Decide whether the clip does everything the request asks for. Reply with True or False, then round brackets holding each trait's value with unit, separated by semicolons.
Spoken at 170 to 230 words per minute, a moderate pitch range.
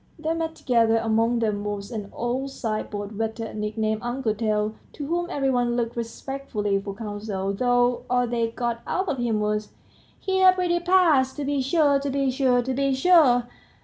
True (180 wpm; 4.1 semitones)